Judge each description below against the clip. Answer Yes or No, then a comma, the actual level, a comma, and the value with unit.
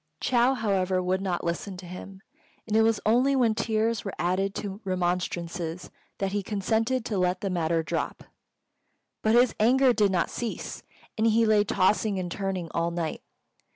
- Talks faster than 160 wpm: Yes, average, 170 wpm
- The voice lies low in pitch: No, high, 195 Hz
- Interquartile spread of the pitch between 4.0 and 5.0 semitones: No, average, 3.4 semitones